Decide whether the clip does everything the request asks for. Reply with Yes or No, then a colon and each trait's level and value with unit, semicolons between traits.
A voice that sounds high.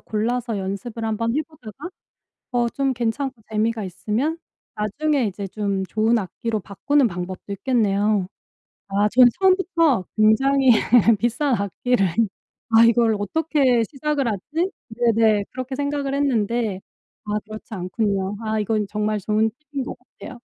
Yes: high, 225 Hz